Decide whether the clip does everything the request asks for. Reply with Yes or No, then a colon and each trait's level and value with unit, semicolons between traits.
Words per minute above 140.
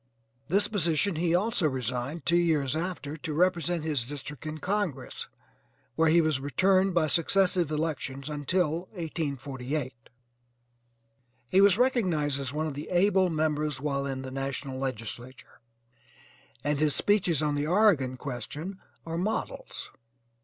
No: slow, 135 wpm